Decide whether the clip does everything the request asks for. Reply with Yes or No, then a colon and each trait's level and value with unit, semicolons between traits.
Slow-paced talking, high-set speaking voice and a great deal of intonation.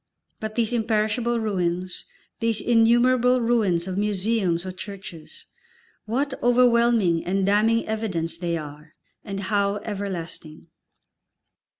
No: slow, 105 wpm; high, 210 Hz; average, 4.2 semitones